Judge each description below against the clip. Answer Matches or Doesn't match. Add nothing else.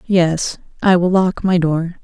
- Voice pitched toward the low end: Doesn't match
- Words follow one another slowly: Doesn't match